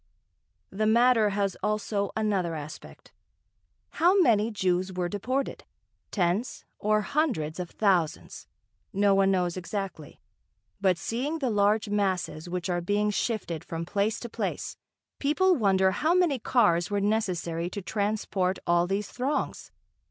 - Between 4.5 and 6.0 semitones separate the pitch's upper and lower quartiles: No, average, 3.4 semitones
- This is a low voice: No, high, 200 Hz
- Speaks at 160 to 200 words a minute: No, slow, 135 wpm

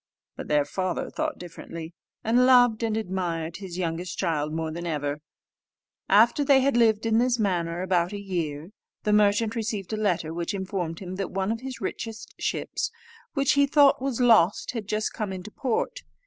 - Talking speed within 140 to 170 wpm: No, average, 180 wpm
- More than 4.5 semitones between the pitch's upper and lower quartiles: Yes, average, 4.9 semitones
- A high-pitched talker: Yes, high, 200 Hz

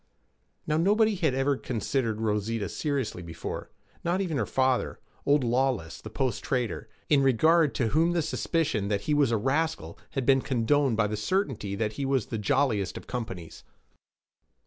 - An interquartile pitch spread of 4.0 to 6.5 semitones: Yes, average, 5.3 semitones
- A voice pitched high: No, low, 130 Hz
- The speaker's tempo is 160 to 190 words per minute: Yes, average, 170 wpm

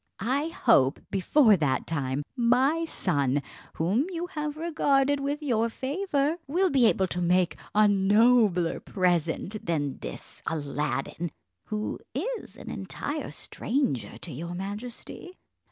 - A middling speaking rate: No, slow, 125 wpm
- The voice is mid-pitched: No, high, 215 Hz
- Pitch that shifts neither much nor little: No, wide, 8.8 semitones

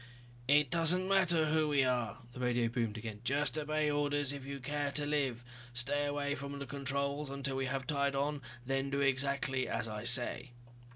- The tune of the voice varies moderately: No, narrow, 2.2 semitones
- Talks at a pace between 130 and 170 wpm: No, average, 185 wpm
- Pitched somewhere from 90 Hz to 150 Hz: Yes, medium, 140 Hz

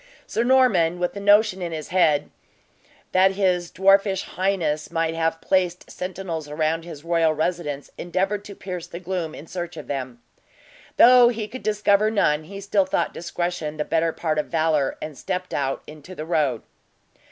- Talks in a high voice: No, medium, 175 Hz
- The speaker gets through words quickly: No, average, 170 wpm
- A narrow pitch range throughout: No, average, 3.5 semitones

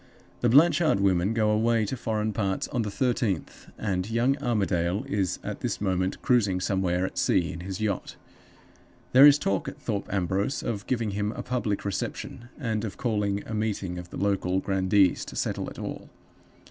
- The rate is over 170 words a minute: Yes, average, 180 wpm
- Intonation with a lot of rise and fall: No, average, 3.3 semitones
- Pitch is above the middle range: No, low, 105 Hz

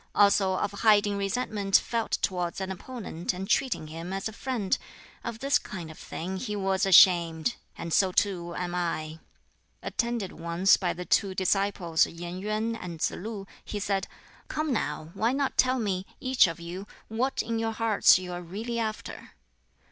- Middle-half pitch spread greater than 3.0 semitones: Yes, average, 4.0 semitones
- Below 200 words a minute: Yes, average, 170 wpm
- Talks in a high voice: Yes, high, 195 Hz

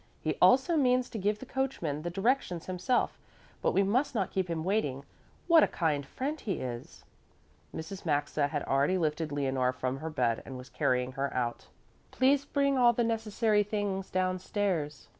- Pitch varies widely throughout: Yes, wide, 8.2 semitones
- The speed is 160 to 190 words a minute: Yes, average, 175 wpm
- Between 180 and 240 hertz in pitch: Yes, medium, 185 Hz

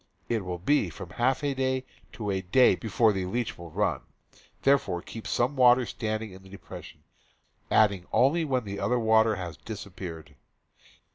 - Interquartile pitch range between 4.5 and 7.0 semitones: Yes, average, 5.0 semitones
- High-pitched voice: No, low, 110 Hz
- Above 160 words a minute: Yes, average, 170 wpm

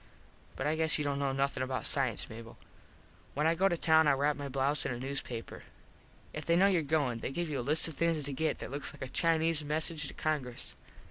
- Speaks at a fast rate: Yes, fast, 240 wpm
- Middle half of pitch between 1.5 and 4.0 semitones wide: Yes, average, 2.9 semitones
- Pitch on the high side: No, medium, 145 Hz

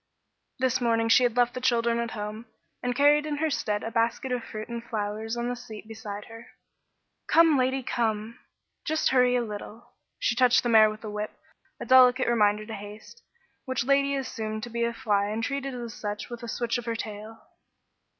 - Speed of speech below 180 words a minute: No, average, 200 wpm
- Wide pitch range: No, narrow, 2.6 semitones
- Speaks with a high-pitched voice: Yes, high, 235 Hz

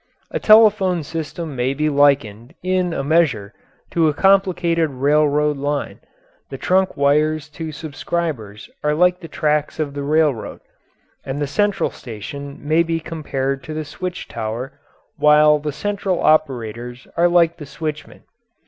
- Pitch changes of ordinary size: Yes, average, 3.2 semitones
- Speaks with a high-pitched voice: No, medium, 150 Hz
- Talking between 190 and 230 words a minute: No, average, 145 wpm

